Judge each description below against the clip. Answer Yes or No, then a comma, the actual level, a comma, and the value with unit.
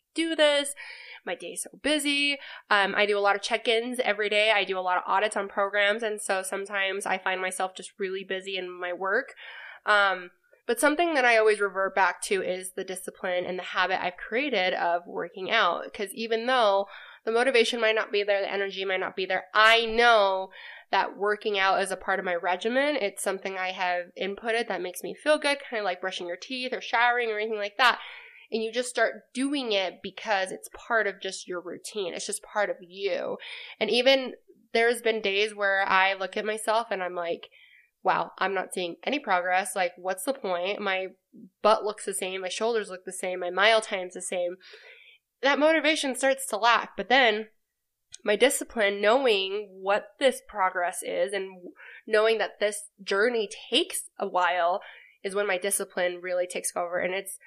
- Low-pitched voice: No, high, 205 Hz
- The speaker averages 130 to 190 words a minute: No, average, 200 wpm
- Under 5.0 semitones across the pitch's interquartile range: Yes, average, 4.1 semitones